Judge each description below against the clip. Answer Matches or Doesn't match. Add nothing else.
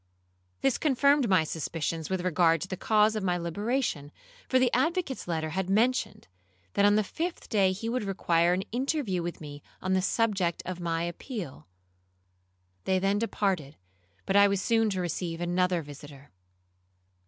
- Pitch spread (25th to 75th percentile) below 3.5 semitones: Doesn't match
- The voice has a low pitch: Doesn't match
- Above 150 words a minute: Matches